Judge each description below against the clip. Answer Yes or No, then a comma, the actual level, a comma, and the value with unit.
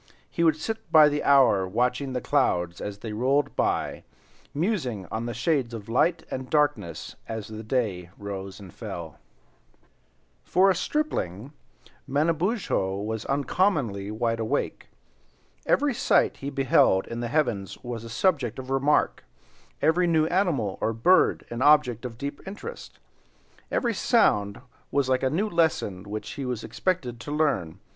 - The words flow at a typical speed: Yes, average, 150 wpm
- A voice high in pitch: No, low, 130 Hz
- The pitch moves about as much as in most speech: No, wide, 6.4 semitones